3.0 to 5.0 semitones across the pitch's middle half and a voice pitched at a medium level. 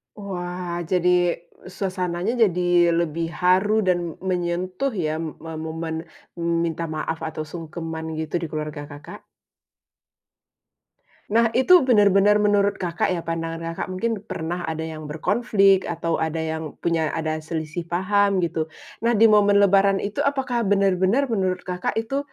Yes: average, 3.8 semitones; medium, 180 Hz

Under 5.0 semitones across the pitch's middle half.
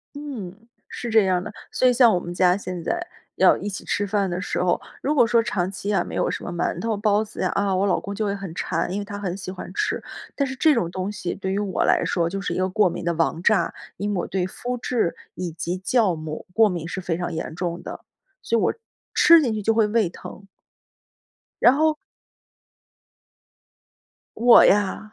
Yes: average, 3.7 semitones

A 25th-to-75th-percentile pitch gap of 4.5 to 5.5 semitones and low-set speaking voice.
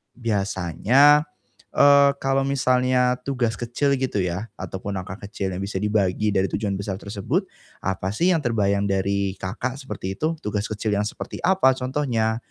Yes: average, 5.0 semitones; low, 110 Hz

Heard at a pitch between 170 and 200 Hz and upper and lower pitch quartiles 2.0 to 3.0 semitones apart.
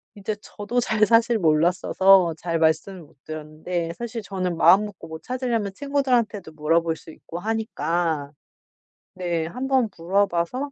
No: medium, 185 Hz; average, 5.2 semitones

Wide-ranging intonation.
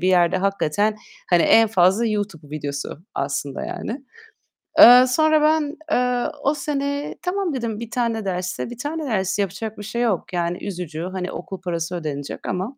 Yes: wide, 5.8 semitones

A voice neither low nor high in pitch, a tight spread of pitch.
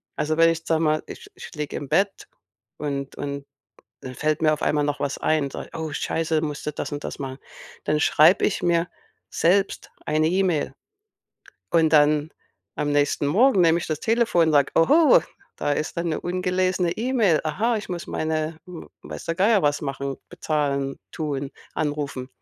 No: medium, 155 Hz; average, 3.3 semitones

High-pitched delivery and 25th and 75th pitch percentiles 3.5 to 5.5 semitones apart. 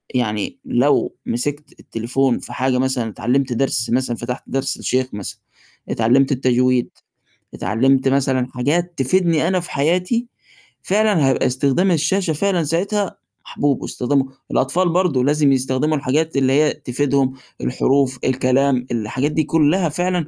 No: low, 135 Hz; average, 3.9 semitones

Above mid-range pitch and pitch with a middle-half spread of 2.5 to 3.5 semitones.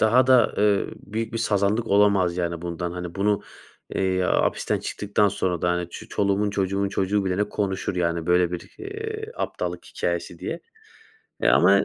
No: low, 100 Hz; average, 2.8 semitones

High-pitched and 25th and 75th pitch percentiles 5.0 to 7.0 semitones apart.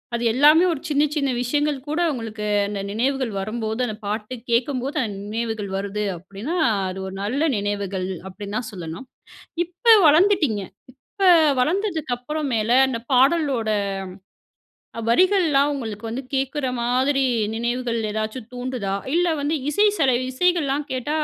Yes: very high, 250 Hz; average, 5.3 semitones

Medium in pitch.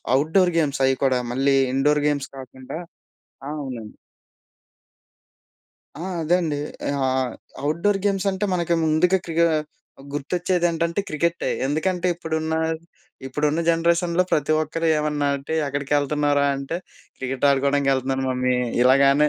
Yes: medium, 150 Hz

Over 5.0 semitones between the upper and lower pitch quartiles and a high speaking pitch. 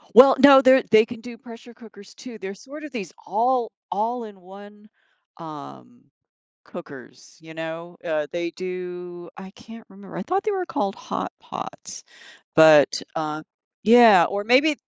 Yes: wide, 5.6 semitones; high, 205 Hz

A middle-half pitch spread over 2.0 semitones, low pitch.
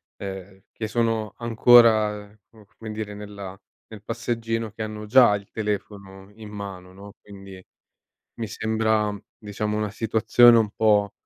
No: narrow, 1.7 semitones; low, 105 Hz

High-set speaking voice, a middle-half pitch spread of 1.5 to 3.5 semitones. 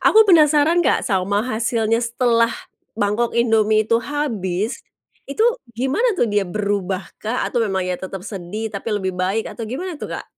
No: high, 225 Hz; average, 4.2 semitones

